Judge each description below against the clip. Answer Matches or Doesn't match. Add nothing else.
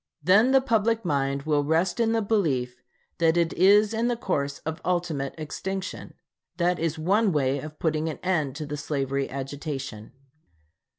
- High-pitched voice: Doesn't match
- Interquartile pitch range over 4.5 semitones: Matches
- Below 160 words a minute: Doesn't match